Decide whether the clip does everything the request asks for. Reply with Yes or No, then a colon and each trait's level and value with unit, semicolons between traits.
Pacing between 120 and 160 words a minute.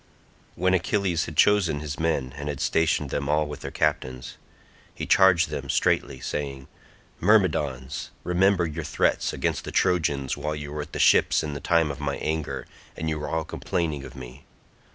No: average, 180 wpm